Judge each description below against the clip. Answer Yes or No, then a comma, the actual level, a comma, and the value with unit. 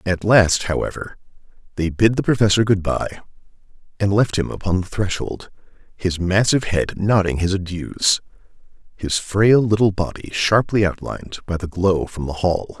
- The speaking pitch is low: Yes, very low, 95 Hz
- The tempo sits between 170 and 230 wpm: No, average, 155 wpm